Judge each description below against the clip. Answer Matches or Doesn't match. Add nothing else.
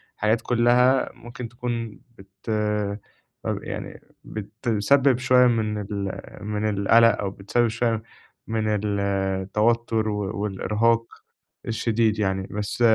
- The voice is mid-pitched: Doesn't match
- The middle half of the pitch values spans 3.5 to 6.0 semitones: Doesn't match